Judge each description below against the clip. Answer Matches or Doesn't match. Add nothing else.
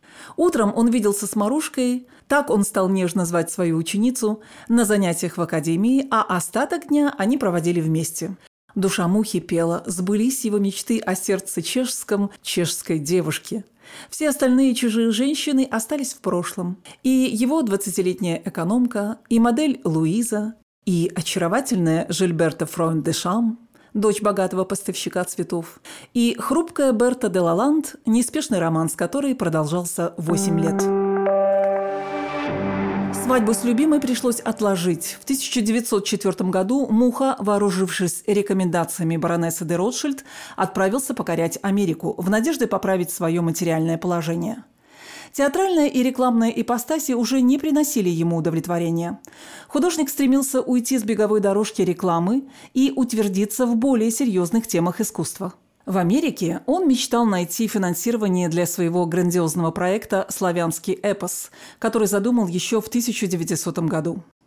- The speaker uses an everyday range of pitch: Doesn't match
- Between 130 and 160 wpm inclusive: Doesn't match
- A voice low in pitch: Doesn't match